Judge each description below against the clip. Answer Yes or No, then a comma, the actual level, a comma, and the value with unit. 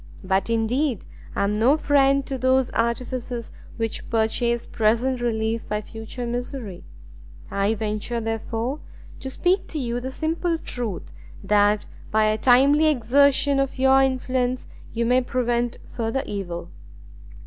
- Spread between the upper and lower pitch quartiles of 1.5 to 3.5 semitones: Yes, average, 3.2 semitones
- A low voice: No, high, 240 Hz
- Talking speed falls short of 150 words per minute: Yes, slow, 135 wpm